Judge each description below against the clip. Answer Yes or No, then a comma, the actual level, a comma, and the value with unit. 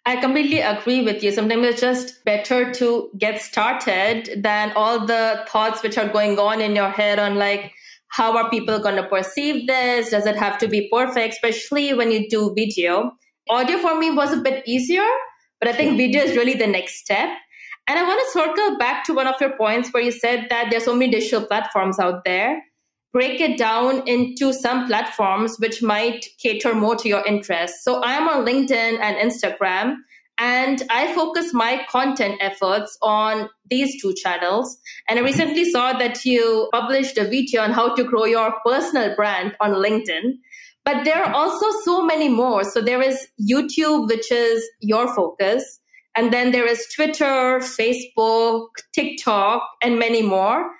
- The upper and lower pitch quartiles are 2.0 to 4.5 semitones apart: Yes, average, 3.4 semitones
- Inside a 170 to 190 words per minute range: Yes, average, 180 wpm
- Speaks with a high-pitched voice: Yes, high, 235 Hz